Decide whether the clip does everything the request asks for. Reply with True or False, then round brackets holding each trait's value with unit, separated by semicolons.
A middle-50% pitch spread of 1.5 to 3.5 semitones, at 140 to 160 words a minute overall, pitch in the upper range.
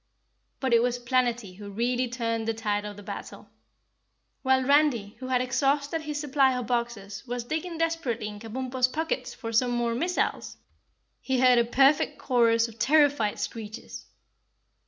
True (2.9 semitones; 155 wpm; 245 Hz)